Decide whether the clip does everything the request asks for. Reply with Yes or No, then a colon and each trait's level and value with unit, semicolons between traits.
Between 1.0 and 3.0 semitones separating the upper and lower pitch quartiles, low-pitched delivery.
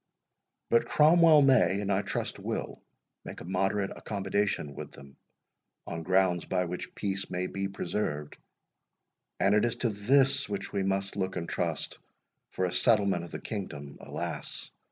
Yes: narrow, 2.4 semitones; very low, 95 Hz